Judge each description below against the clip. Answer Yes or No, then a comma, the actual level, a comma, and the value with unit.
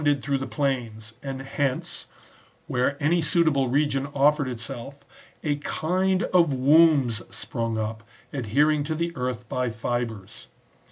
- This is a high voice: No, low, 135 Hz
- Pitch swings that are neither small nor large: Yes, average, 3.8 semitones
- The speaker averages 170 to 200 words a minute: No, slow, 135 wpm